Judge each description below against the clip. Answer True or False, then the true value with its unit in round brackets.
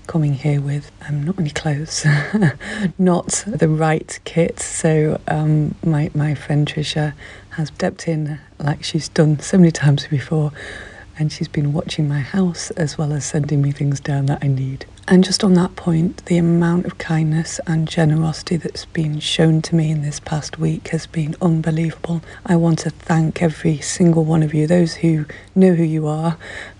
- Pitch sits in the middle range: True (160 Hz)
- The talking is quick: False (180 wpm)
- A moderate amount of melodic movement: False (2.1 semitones)